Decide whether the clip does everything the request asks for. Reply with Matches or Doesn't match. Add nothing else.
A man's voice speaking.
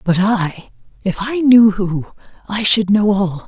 Doesn't match